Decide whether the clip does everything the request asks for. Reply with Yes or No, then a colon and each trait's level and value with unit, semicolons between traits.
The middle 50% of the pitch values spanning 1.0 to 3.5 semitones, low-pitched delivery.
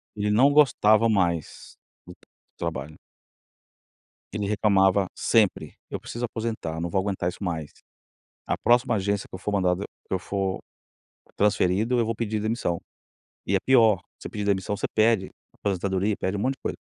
Yes: average, 2.8 semitones; low, 100 Hz